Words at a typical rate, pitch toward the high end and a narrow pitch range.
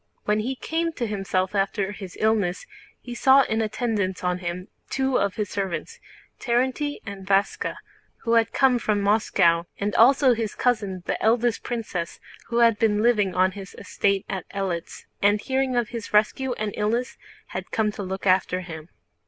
No: average, 170 wpm; high, 210 Hz; average, 3.9 semitones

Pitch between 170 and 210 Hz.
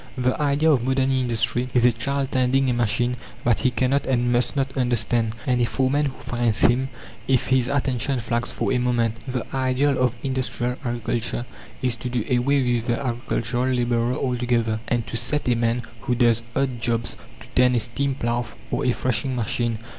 No: low, 125 Hz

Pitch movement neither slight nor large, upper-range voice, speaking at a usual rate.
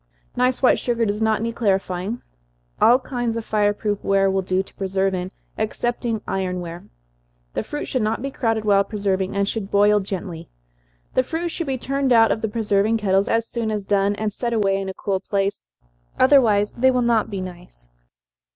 Yes: average, 3.2 semitones; high, 210 Hz; average, 195 wpm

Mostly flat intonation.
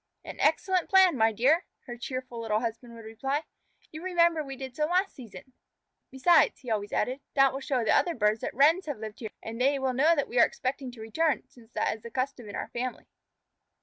No: average, 4.7 semitones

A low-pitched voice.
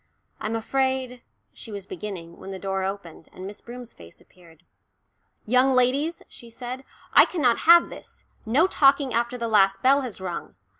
No: high, 235 Hz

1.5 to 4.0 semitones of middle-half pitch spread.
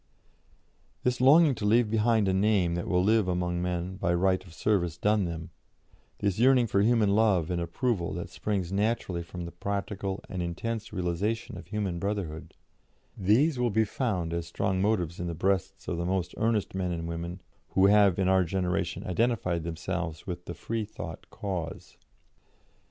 Yes: average, 3.6 semitones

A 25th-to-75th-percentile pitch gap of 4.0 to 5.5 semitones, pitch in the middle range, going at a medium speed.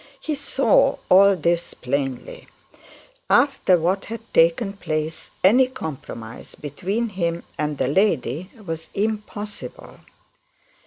No: average, 5.2 semitones; medium, 180 Hz; slow, 105 wpm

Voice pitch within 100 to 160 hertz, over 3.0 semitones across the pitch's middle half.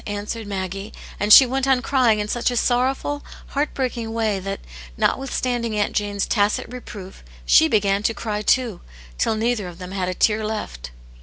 No: high, 215 Hz; average, 3.5 semitones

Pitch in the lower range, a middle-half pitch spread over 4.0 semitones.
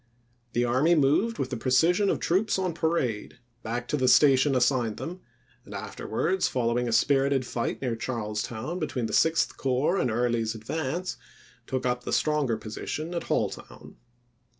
Yes: low, 130 Hz; average, 5.1 semitones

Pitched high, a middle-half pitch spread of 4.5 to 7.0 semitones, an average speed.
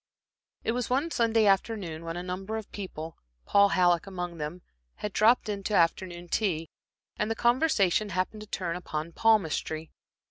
No: high, 195 Hz; average, 4.1 semitones; average, 165 wpm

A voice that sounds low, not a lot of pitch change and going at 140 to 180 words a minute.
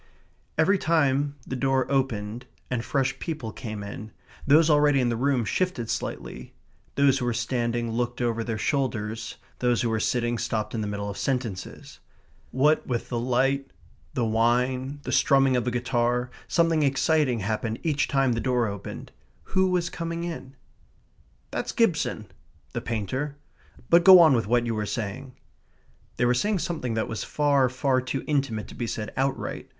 No: low, 125 Hz; average, 3.5 semitones; average, 170 wpm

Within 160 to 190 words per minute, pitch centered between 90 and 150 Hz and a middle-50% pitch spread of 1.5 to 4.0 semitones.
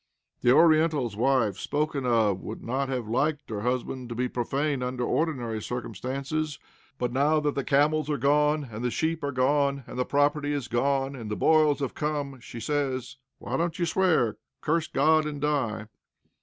Yes: average, 180 wpm; medium, 140 Hz; average, 3.3 semitones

